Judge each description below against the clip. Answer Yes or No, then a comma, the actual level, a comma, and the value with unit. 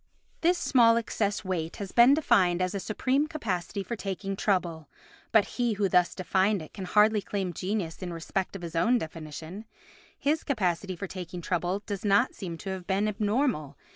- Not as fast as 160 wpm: No, average, 175 wpm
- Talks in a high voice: Yes, high, 195 Hz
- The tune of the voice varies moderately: Yes, average, 3.6 semitones